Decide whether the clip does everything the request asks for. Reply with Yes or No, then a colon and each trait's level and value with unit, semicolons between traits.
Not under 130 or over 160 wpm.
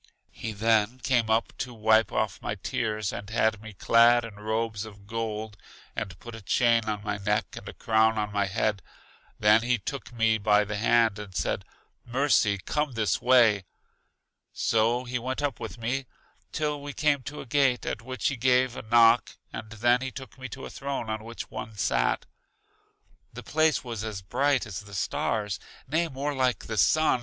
No: average, 190 wpm